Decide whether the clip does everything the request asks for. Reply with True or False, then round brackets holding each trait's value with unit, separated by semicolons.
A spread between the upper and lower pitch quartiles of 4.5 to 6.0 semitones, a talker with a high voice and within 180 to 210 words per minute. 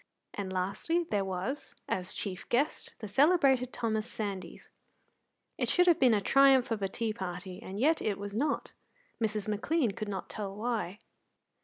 False (5.3 semitones; 215 Hz; 165 wpm)